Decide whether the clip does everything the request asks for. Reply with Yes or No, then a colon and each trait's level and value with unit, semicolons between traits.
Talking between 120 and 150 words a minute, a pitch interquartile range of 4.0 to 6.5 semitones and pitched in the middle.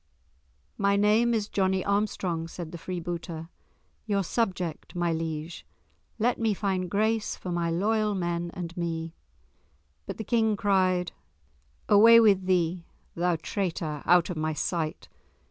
No: slow, 135 wpm; average, 3.5 semitones; medium, 180 Hz